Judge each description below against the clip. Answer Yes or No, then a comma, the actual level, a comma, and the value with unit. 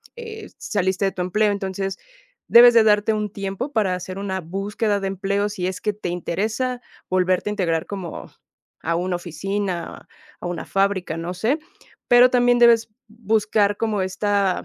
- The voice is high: Yes, high, 200 Hz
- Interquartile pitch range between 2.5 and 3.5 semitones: Yes, average, 2.8 semitones